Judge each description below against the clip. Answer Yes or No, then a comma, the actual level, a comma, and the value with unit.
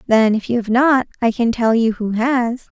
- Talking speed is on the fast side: Yes, fast, 235 wpm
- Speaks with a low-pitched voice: No, high, 235 Hz